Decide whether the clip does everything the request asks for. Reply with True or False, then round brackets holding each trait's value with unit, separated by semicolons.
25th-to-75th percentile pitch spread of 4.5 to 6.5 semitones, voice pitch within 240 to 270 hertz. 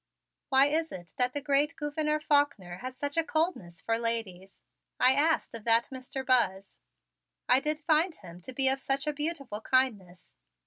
True (4.8 semitones; 265 Hz)